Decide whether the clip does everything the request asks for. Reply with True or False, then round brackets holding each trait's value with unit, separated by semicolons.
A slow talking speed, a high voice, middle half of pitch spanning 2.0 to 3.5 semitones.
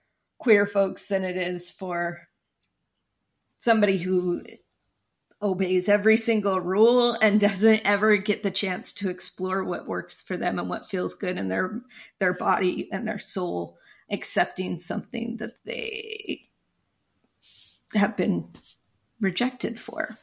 True (130 wpm; 200 Hz; 3.1 semitones)